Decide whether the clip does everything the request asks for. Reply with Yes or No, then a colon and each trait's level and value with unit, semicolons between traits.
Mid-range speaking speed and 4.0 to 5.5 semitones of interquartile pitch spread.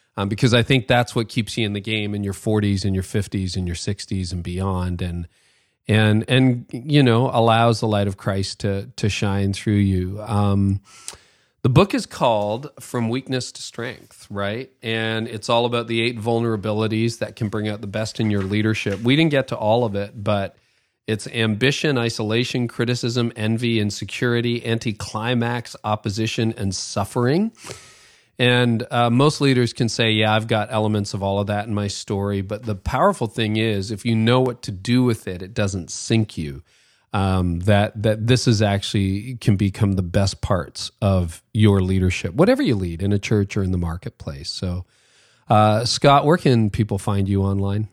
No: average, 185 wpm; average, 3.0 semitones